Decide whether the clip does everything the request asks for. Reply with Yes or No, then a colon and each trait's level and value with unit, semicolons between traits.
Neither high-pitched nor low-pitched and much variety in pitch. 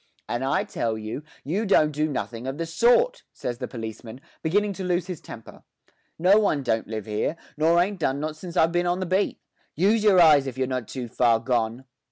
Yes: medium, 150 Hz; wide, 6.7 semitones